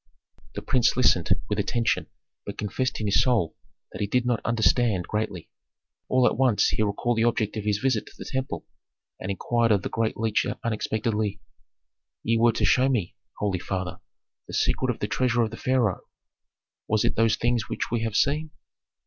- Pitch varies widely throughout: No, average, 2.8 semitones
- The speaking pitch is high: No, low, 115 Hz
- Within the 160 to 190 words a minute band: Yes, average, 185 wpm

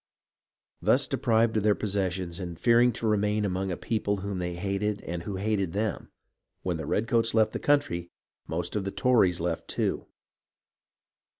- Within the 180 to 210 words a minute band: No, average, 165 wpm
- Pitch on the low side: Yes, low, 100 Hz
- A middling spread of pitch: Yes, average, 3.5 semitones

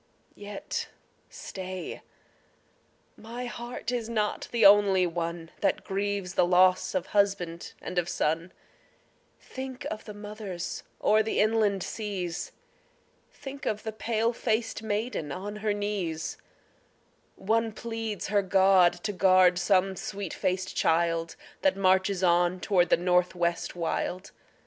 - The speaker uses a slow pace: Yes, slow, 130 wpm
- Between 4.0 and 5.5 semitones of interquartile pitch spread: No, average, 3.2 semitones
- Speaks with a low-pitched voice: No, high, 195 Hz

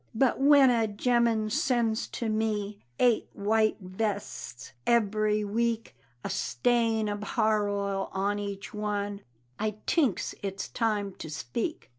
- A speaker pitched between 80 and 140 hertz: No, high, 215 Hz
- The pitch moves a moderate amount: No, narrow, 2.3 semitones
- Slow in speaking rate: Yes, slow, 130 wpm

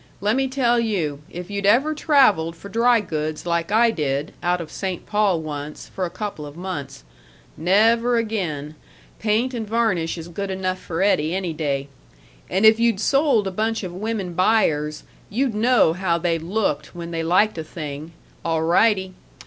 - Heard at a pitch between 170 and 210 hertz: Yes, medium, 185 Hz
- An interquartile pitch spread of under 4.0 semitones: No, average, 5.3 semitones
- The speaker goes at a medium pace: Yes, average, 175 wpm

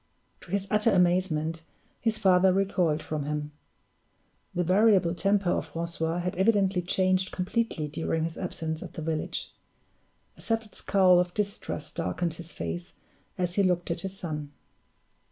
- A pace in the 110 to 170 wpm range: Yes, average, 150 wpm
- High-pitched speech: No, medium, 180 Hz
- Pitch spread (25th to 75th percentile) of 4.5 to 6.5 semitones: No, average, 3.0 semitones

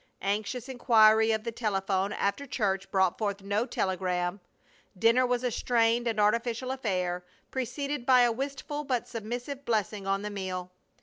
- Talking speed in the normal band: Yes, average, 150 wpm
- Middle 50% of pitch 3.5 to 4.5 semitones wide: Yes, average, 4.0 semitones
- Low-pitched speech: No, high, 220 Hz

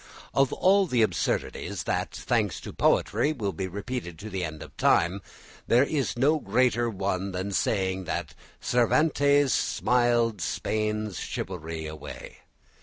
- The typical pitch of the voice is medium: No, low, 105 Hz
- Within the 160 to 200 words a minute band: No, slow, 135 wpm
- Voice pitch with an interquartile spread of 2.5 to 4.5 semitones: No, average, 5.1 semitones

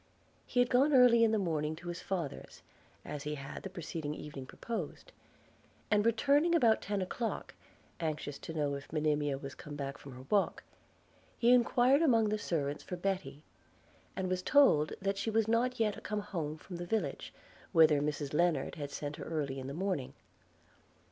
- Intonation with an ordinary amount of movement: No, wide, 7.0 semitones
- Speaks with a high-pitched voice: No, medium, 175 Hz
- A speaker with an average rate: Yes, average, 180 wpm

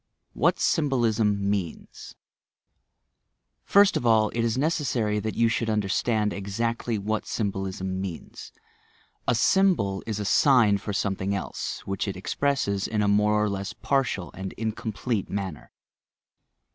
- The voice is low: Yes, low, 105 Hz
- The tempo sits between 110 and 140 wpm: Yes, slow, 135 wpm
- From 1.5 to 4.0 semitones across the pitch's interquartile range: Yes, average, 2.9 semitones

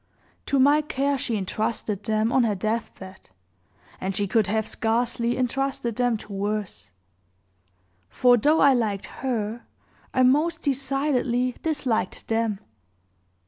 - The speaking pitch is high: Yes, high, 235 Hz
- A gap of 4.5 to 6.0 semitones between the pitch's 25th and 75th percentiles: No, average, 3.8 semitones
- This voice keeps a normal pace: No, slow, 125 wpm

